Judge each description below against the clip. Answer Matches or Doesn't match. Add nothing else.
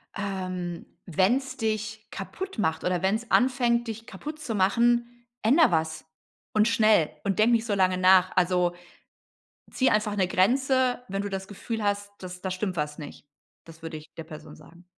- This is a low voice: Doesn't match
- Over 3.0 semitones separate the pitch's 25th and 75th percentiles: Matches